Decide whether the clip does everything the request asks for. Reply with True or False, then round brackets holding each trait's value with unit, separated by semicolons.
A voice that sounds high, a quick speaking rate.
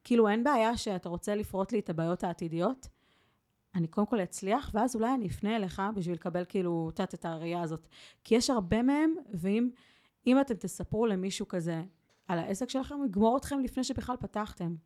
True (205 Hz; 180 wpm)